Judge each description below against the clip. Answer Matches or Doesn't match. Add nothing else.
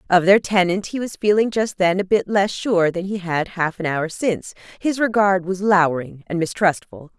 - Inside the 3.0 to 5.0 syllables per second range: Matches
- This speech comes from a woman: Matches